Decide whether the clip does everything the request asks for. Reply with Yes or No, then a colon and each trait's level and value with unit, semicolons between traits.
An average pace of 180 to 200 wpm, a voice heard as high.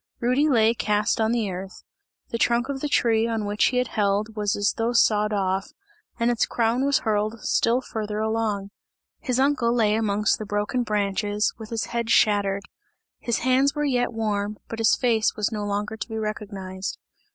Yes: average, 185 wpm; high, 220 Hz